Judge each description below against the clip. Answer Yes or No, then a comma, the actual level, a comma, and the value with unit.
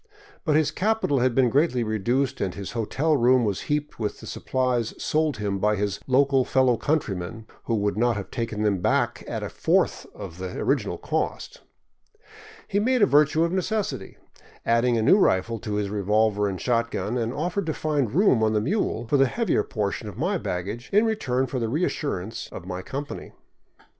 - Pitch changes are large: Yes, wide, 5.9 semitones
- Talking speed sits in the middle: Yes, average, 195 wpm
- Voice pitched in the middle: No, low, 120 Hz